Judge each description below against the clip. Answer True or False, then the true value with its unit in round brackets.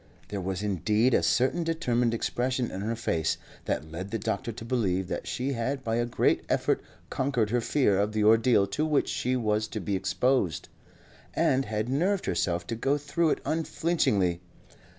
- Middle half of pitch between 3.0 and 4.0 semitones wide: False (4.6 semitones)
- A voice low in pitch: True (115 Hz)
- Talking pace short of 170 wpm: False (180 wpm)